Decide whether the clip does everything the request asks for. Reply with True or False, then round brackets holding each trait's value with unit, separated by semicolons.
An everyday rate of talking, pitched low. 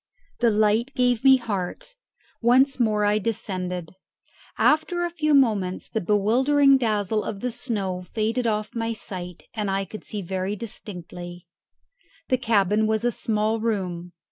False (145 wpm; 215 Hz)